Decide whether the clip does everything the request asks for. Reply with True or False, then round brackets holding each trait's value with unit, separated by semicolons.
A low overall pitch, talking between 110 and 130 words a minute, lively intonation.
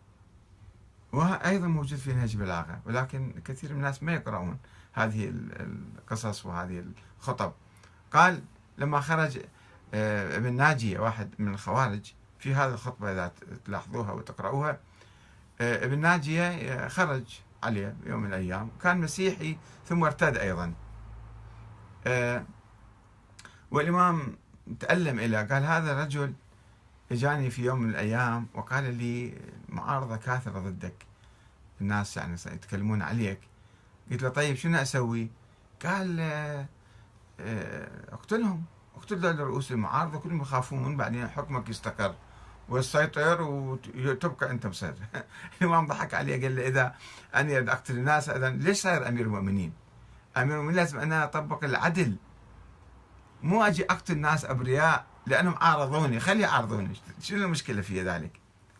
True (120 Hz; 115 wpm; 6.0 semitones)